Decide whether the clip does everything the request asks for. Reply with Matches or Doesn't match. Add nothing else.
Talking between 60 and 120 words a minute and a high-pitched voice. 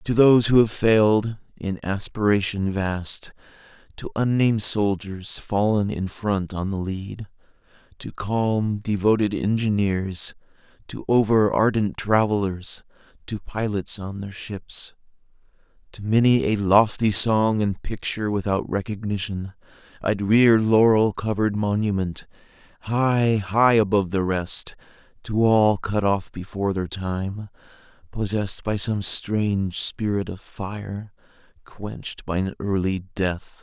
Doesn't match